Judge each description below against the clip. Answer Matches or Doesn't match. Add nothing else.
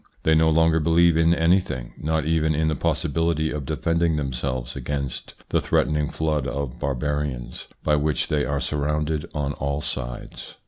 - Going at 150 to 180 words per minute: Matches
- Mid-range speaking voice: Doesn't match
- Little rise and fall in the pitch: Matches